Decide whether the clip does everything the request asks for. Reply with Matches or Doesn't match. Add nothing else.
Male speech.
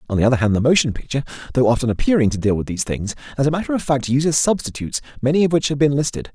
Matches